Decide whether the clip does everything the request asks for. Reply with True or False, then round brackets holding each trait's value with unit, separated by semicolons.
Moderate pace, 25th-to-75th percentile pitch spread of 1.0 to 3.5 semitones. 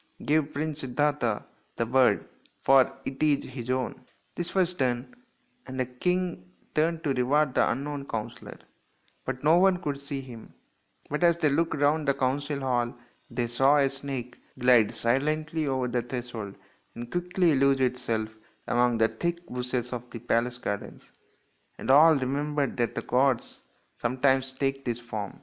True (160 wpm; 3.2 semitones)